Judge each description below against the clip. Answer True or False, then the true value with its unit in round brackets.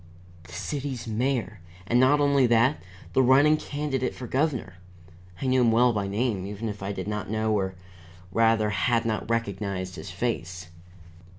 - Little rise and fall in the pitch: False (4.2 semitones)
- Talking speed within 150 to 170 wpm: True (165 wpm)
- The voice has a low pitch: True (115 Hz)